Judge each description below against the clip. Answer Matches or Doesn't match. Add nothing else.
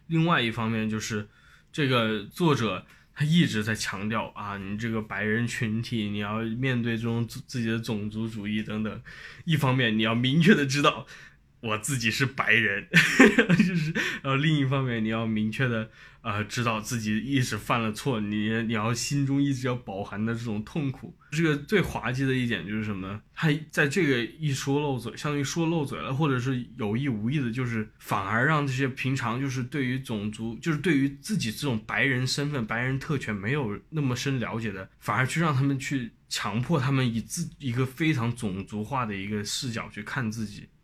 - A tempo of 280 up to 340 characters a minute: Matches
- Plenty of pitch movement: Doesn't match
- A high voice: Doesn't match